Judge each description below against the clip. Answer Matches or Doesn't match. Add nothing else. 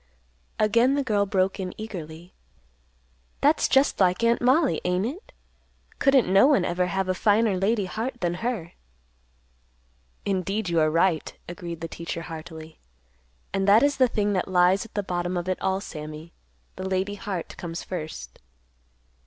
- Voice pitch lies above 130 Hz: Matches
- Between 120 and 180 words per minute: Matches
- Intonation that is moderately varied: Matches